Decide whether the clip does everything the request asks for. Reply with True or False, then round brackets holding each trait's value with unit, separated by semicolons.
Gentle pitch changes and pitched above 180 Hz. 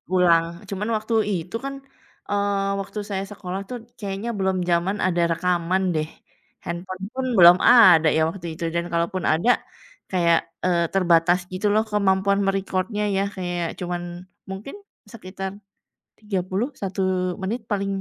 True (2.3 semitones; 190 Hz)